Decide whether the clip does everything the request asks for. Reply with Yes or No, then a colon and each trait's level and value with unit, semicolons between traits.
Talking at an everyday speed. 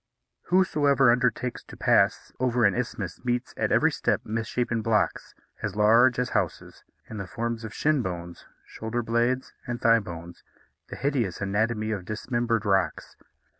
Yes: average, 150 wpm